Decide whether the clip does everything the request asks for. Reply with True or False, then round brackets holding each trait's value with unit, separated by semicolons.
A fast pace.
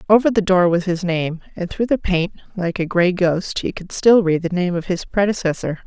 True (235 wpm)